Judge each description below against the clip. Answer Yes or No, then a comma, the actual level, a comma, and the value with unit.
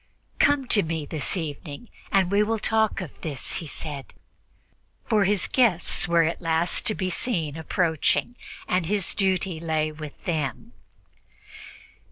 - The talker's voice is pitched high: No, medium, 170 Hz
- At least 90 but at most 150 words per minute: Yes, average, 145 wpm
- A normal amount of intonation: Yes, average, 4.2 semitones